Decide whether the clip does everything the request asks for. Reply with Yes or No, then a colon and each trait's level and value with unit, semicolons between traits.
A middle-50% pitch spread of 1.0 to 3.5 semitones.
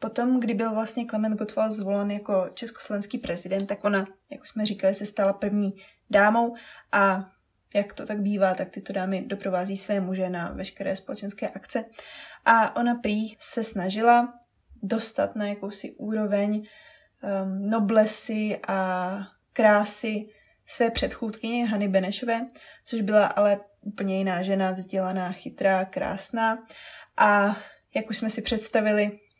Yes: narrow, 2.4 semitones